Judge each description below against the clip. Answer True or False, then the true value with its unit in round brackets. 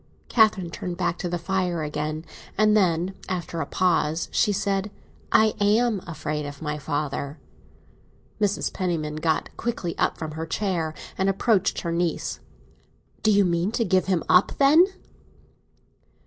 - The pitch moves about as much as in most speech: True (3.9 semitones)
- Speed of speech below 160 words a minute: True (145 wpm)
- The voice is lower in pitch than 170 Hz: False (175 Hz)